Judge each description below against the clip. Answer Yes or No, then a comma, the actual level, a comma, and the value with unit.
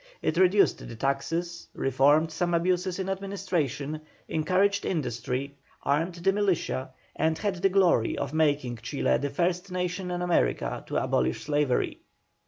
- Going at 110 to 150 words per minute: Yes, average, 140 wpm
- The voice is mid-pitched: Yes, medium, 165 Hz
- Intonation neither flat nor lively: Yes, average, 4.5 semitones